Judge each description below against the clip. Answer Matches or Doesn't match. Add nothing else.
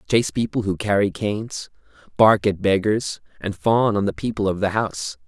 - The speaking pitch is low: Matches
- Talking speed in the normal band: Matches